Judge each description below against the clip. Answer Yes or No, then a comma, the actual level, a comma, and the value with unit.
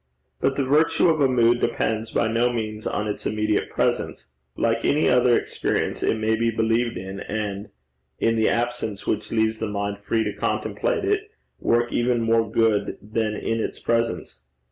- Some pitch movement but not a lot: No, narrow, 2.0 semitones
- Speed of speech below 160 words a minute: No, average, 175 wpm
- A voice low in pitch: Yes, low, 115 Hz